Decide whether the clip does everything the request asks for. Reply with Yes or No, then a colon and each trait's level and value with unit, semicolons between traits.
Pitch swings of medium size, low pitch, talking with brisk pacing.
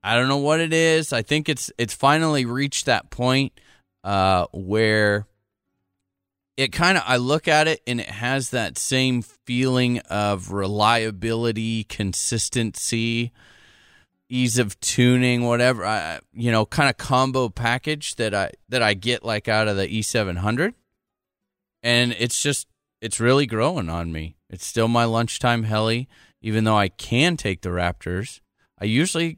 No: average, 3.8 semitones; low, 115 Hz; average, 155 wpm